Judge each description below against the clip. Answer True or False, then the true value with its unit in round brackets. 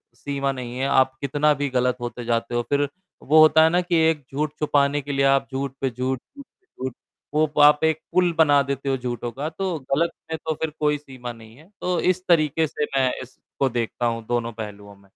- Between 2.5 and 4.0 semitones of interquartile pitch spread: True (3.6 semitones)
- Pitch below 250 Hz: True (140 Hz)